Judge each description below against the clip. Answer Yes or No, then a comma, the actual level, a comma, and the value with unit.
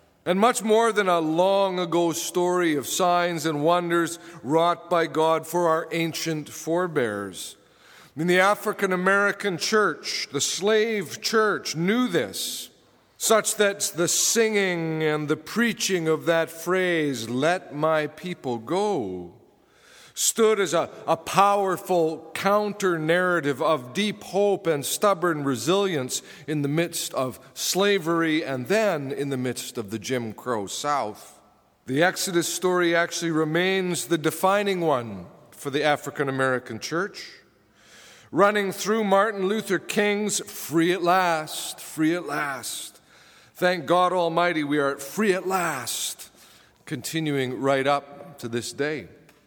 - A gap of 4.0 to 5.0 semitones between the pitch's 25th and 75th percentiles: Yes, average, 4.3 semitones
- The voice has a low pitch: No, medium, 170 Hz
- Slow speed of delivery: Yes, slow, 130 wpm